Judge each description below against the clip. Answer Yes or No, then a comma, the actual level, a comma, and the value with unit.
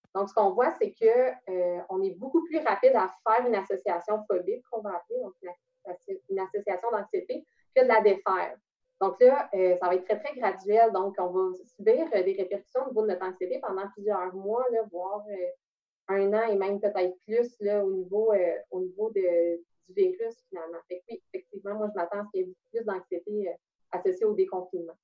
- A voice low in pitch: No, high, 205 Hz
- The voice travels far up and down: Yes, wide, 6.2 semitones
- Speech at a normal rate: Yes, average, 210 wpm